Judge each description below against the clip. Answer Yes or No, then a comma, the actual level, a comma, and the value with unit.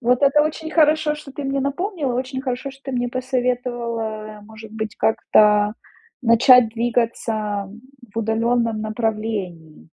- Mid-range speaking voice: No, high, 240 Hz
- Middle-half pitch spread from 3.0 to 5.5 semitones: Yes, average, 3.4 semitones